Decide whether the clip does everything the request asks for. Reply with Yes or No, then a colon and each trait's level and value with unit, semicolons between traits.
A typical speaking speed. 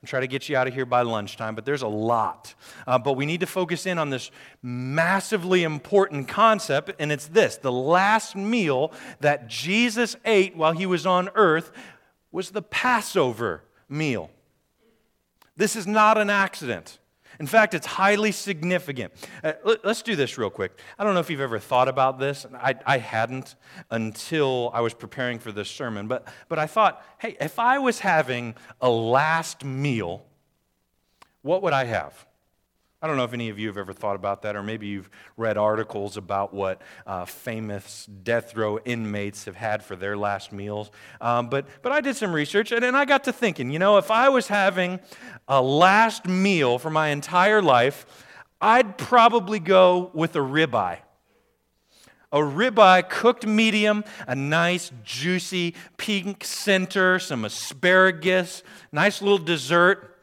Yes: average, 170 wpm